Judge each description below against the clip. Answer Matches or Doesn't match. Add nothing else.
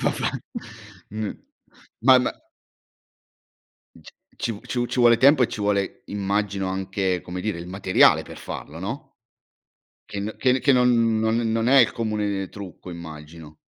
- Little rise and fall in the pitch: Doesn't match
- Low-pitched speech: Matches